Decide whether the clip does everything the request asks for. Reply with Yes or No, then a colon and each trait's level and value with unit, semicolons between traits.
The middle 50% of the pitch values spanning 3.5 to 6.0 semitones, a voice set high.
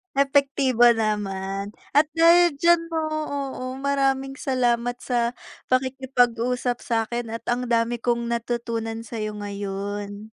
No: average, 3.1 semitones; high, 240 Hz